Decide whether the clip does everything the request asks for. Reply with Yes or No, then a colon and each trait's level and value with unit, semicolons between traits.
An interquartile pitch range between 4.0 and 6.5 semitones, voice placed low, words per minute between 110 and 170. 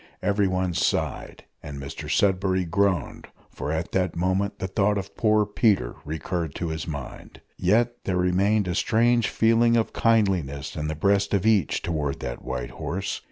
Yes: average, 4.3 semitones; very low, 95 Hz; average, 160 wpm